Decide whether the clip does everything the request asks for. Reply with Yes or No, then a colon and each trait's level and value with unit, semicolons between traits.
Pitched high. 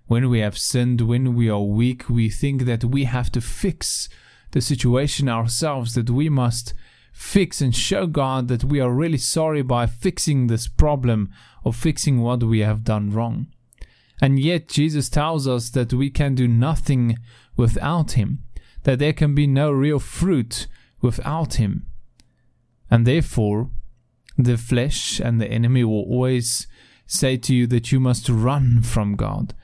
No: low, 125 Hz